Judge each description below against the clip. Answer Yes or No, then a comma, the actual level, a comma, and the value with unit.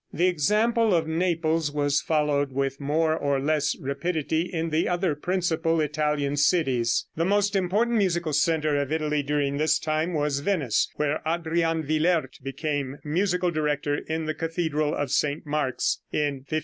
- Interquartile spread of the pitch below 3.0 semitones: Yes, narrow, 2.6 semitones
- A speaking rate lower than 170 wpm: Yes, average, 155 wpm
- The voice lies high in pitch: No, medium, 155 Hz